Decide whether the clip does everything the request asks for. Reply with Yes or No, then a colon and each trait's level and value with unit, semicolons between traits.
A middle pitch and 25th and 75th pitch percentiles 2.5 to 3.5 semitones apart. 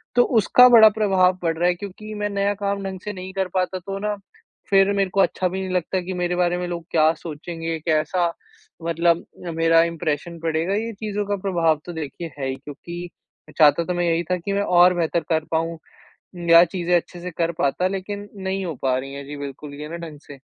Yes: medium, 175 Hz; average, 2.9 semitones